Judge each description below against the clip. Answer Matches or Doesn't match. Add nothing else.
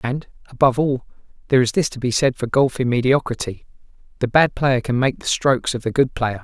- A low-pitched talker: Matches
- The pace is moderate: Doesn't match